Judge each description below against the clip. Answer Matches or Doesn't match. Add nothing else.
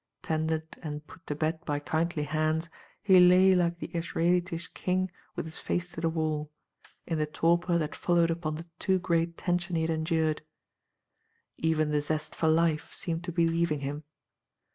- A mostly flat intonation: Matches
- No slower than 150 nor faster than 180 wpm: Matches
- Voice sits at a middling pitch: Matches